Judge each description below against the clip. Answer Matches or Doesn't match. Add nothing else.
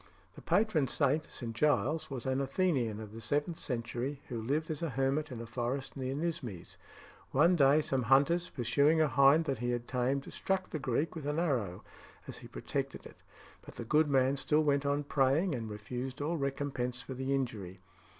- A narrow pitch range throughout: Doesn't match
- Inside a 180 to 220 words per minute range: Matches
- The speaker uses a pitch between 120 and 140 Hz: Matches